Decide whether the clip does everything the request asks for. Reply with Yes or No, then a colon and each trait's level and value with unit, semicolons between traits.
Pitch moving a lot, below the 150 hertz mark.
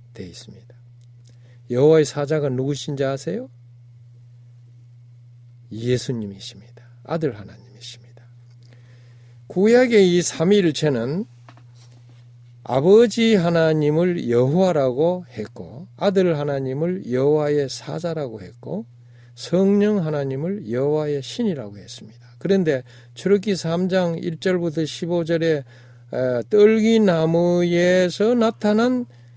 Yes: wide, 6.4 semitones; medium, 140 Hz